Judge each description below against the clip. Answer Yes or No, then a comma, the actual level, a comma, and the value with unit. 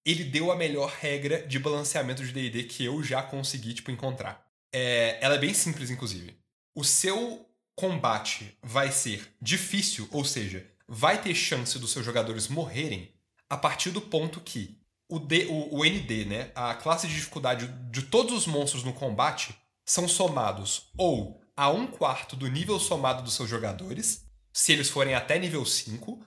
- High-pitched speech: No, low, 135 Hz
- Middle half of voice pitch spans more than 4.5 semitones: Yes, wide, 5.5 semitones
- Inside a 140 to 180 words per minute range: Yes, average, 170 wpm